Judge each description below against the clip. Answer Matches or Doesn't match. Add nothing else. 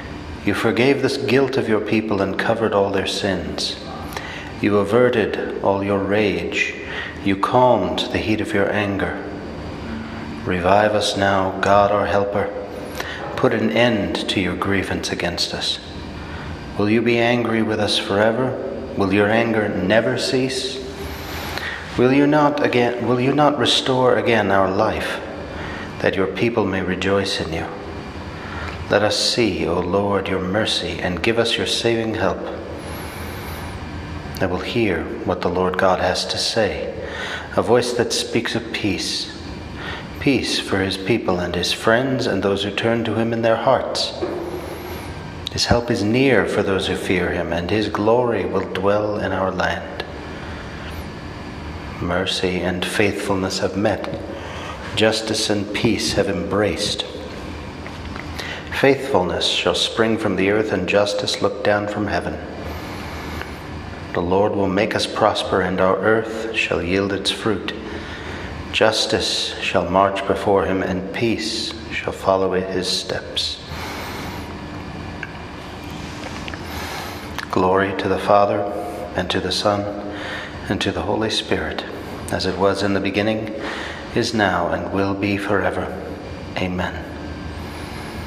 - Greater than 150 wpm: Doesn't match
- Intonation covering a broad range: Doesn't match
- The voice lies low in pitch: Matches